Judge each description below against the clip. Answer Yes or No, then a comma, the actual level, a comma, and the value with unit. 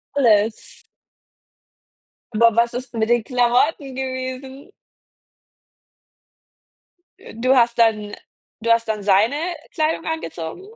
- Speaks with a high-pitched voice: Yes, high, 240 Hz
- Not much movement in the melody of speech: No, average, 3.1 semitones